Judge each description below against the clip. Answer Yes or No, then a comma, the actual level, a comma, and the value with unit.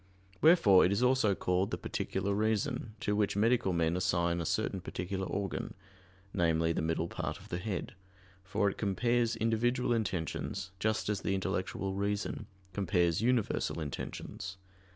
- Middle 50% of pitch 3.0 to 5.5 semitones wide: Yes, average, 3.4 semitones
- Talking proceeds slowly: No, average, 150 wpm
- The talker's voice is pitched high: No, low, 100 Hz